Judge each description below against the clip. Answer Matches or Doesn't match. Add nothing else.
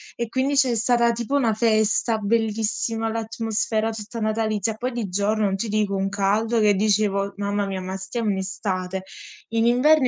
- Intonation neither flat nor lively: Doesn't match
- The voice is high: Matches